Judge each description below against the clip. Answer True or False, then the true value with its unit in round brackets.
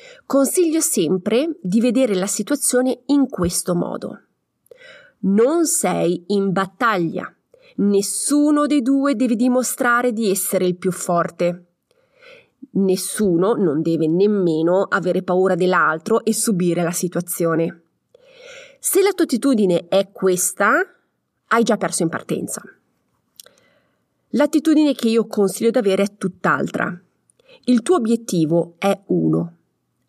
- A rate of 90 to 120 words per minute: True (115 wpm)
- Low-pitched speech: False (215 Hz)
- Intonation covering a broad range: True (7.7 semitones)